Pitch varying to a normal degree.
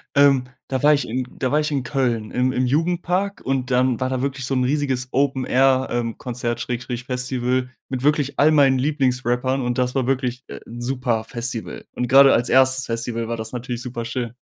No: narrow, 1.8 semitones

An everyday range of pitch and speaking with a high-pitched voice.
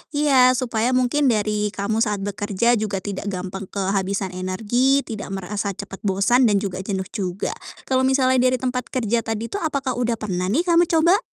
Yes: average, 4.5 semitones; high, 220 Hz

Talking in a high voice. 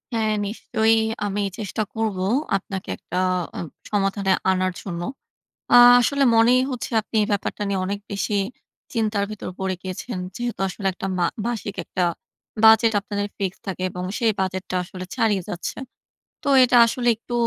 Yes: high, 205 Hz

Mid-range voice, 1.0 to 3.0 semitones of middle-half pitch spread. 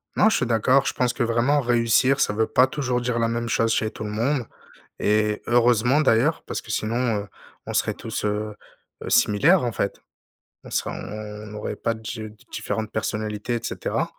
No: low, 115 Hz; narrow, 2.6 semitones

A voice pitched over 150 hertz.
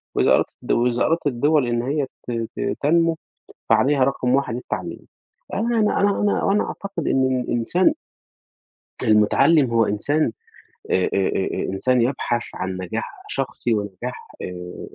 No: low, 125 Hz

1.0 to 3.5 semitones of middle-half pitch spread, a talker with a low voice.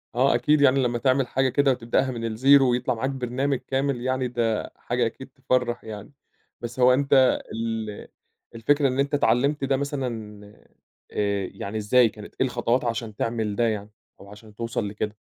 Yes: average, 3.0 semitones; low, 120 Hz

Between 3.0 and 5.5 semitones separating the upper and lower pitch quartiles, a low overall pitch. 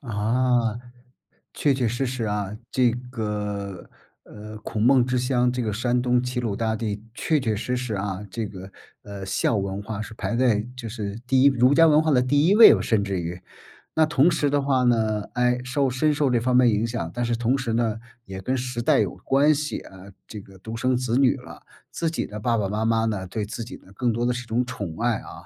Yes: average, 3.3 semitones; low, 120 Hz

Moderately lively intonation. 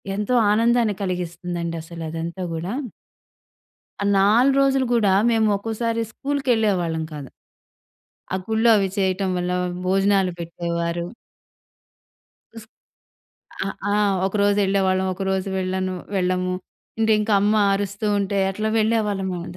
Yes: average, 3.1 semitones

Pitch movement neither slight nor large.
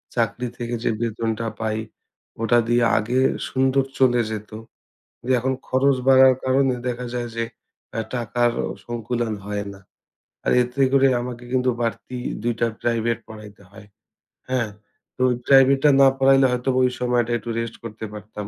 No: narrow, 2.3 semitones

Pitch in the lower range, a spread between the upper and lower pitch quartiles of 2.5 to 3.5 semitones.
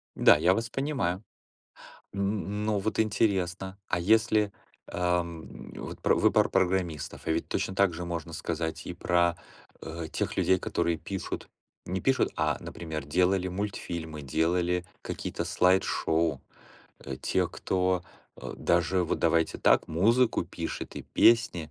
Yes: very low, 90 Hz; average, 2.9 semitones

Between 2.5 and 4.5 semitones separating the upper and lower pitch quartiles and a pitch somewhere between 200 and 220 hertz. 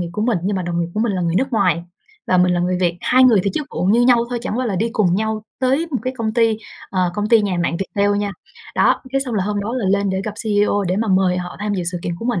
Yes: average, 4.0 semitones; high, 205 Hz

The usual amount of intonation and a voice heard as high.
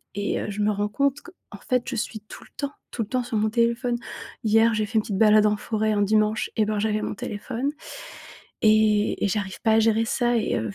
No: narrow, 1.8 semitones; high, 215 Hz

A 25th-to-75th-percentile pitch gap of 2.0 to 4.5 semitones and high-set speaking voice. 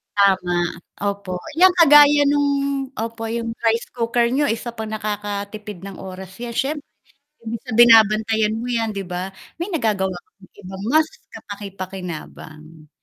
Yes: average, 3.6 semitones; high, 215 Hz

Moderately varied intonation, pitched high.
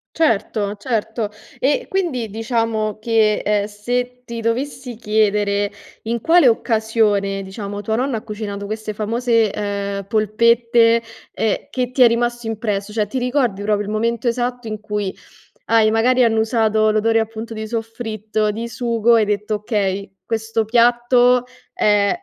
No: narrow, 2.0 semitones; high, 225 Hz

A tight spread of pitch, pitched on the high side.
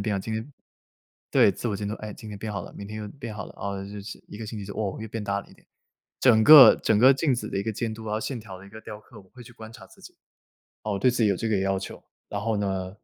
No: narrow, 2.0 semitones; low, 105 Hz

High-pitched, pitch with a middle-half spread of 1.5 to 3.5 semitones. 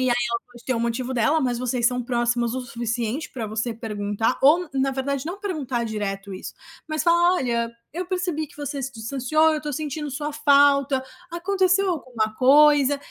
No: very high, 265 Hz; average, 4.3 semitones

